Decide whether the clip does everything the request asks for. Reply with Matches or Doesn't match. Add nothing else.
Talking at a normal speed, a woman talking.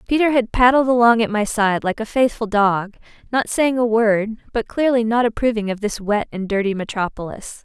Matches